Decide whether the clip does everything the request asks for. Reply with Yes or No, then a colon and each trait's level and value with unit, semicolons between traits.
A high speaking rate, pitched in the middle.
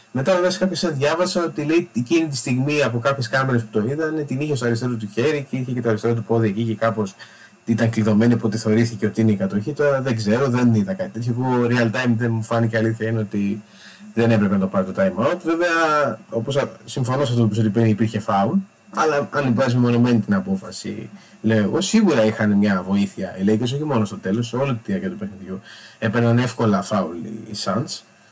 No: fast, 220 wpm; low, 115 Hz